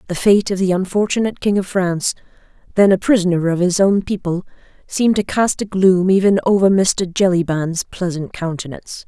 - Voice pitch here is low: No, medium, 185 Hz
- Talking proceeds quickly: No, average, 170 wpm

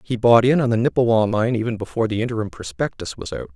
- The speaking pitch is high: No, low, 115 Hz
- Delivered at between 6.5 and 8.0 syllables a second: Yes, 6.7 syllables/s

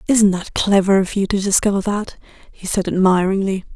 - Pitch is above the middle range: Yes, high, 195 Hz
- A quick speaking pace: No, average, 175 wpm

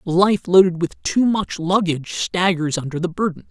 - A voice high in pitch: No, medium, 170 Hz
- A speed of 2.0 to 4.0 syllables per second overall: No, 4.7 syllables/s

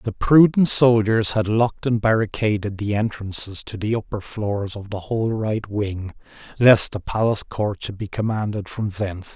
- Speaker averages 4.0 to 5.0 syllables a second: Yes, 4.8 syllables/s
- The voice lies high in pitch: No, low, 105 Hz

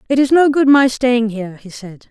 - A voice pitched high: Yes, high, 245 Hz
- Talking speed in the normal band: No, fast, 255 wpm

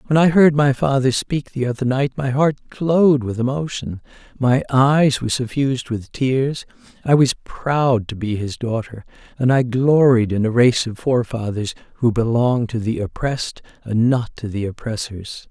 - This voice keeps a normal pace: Yes, average, 175 wpm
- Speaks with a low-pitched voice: Yes, low, 125 Hz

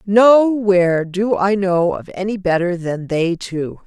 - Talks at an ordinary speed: Yes, average, 155 wpm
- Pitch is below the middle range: No, high, 190 Hz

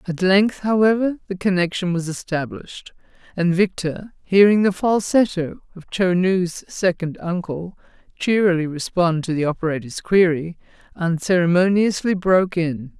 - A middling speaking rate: No, slow, 120 wpm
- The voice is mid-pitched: Yes, medium, 180 Hz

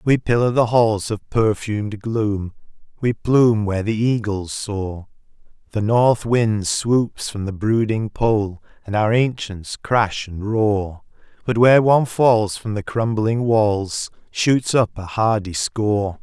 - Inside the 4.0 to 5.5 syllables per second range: No, 3.8 syllables/s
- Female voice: No, male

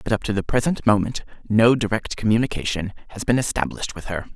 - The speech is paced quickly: No, average, 195 wpm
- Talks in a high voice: No, low, 110 Hz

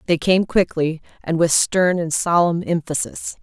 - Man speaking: No, female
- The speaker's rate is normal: Yes, average, 160 wpm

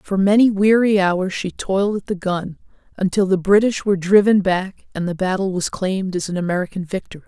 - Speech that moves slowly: No, average, 200 wpm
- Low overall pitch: No, high, 190 Hz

